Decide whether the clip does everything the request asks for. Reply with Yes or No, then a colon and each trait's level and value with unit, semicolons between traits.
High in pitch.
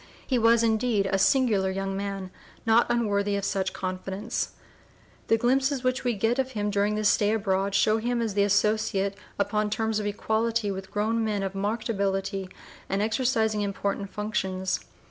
Yes: high, 210 Hz